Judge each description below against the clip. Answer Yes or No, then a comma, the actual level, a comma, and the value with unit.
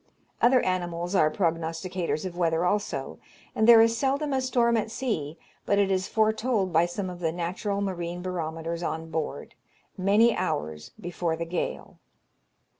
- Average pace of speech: Yes, average, 155 wpm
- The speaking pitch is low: No, medium, 180 Hz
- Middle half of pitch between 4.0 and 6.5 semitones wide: Yes, average, 4.5 semitones